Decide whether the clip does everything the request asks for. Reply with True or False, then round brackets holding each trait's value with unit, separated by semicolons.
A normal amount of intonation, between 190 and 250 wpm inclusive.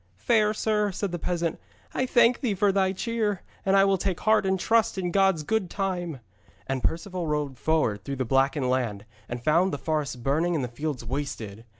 False (6.4 semitones; 200 wpm)